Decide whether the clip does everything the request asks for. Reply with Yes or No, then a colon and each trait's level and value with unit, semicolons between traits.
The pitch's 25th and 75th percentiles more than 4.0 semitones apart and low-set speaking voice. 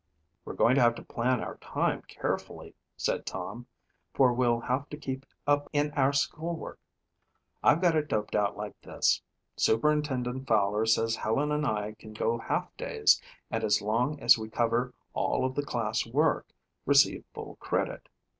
Yes: average, 4.4 semitones; low, 125 Hz